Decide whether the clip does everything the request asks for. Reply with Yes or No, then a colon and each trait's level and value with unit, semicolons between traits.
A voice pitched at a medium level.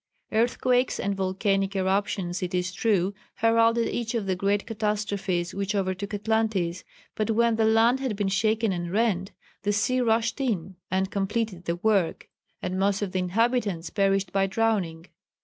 No: high, 200 Hz